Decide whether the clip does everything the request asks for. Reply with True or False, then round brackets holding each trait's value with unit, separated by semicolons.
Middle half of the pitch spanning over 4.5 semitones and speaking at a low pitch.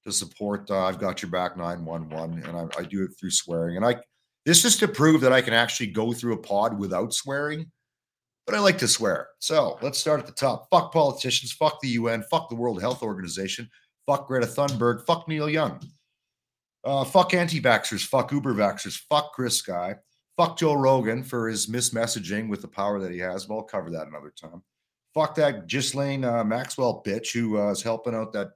True (5.4 semitones; 120 Hz)